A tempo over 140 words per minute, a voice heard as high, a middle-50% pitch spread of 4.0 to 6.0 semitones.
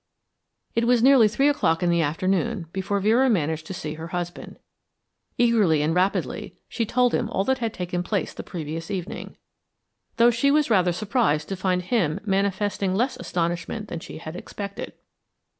Yes: average, 170 wpm; high, 195 Hz; average, 5.1 semitones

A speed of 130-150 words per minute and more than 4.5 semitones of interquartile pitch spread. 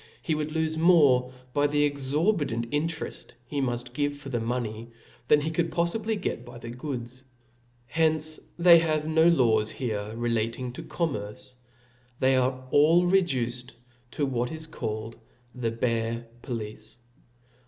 Yes: average, 145 wpm; average, 4.9 semitones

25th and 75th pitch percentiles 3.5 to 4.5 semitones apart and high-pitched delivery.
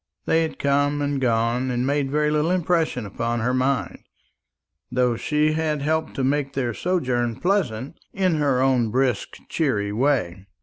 No: average, 3.8 semitones; low, 135 Hz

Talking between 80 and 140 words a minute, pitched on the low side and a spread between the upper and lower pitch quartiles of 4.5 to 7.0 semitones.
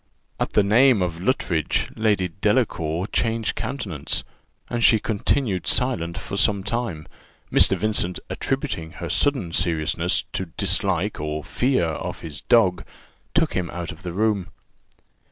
Yes: slow, 135 wpm; very low, 95 Hz; average, 4.8 semitones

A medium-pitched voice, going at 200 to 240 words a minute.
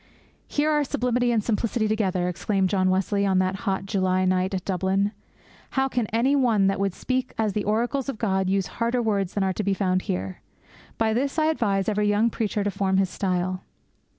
No: high, 200 Hz; fast, 205 wpm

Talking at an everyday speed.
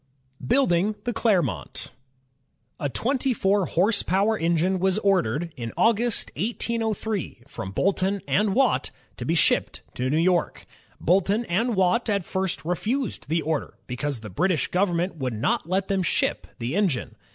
Yes: average, 150 wpm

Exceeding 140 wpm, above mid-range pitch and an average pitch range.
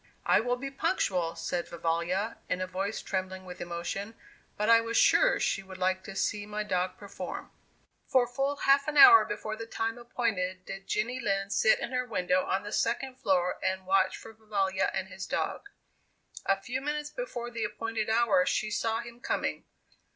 Yes: average, 185 wpm; high, 210 Hz; average, 4.3 semitones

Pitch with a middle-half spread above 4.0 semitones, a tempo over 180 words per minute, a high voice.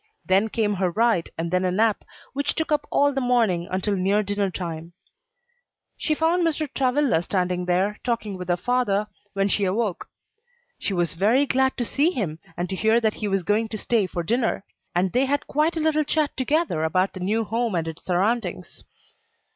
Yes: wide, 5.6 semitones; average, 195 wpm; high, 210 Hz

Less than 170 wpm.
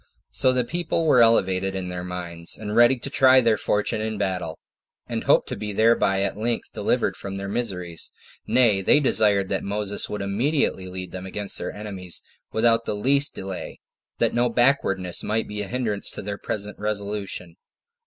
No: average, 185 wpm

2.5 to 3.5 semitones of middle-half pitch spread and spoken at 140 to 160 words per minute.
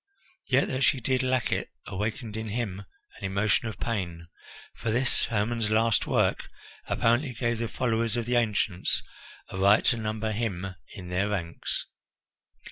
Yes: average, 3.0 semitones; average, 155 wpm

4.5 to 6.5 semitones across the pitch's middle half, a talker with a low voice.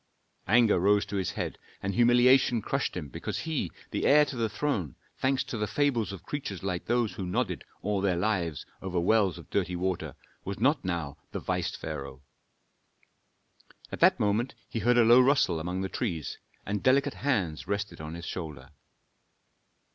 Yes: wide, 5.6 semitones; low, 100 Hz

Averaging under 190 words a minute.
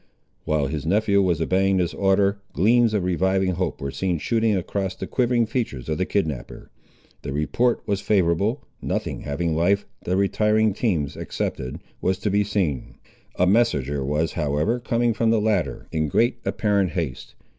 Yes: average, 165 wpm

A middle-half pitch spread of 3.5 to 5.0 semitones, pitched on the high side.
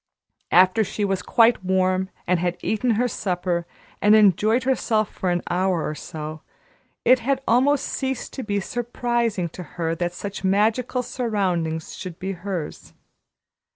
Yes: average, 4.7 semitones; high, 195 Hz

